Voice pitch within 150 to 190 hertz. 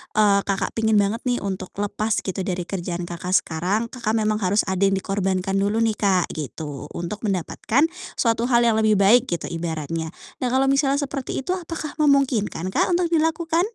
No: high, 210 Hz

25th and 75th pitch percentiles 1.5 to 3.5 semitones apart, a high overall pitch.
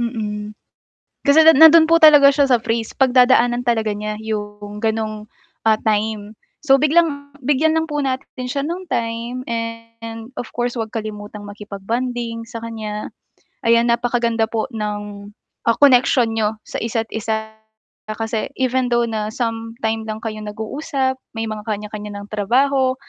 Yes: average, 3.1 semitones; high, 230 Hz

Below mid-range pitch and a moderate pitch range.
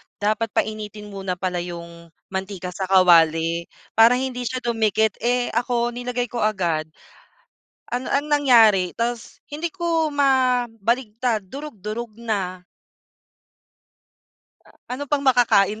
No: high, 225 Hz; average, 4.6 semitones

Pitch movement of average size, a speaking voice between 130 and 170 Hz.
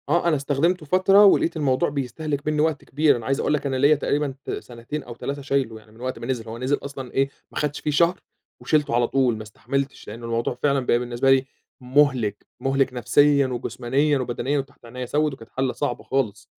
Yes: average, 3.1 semitones; low, 135 Hz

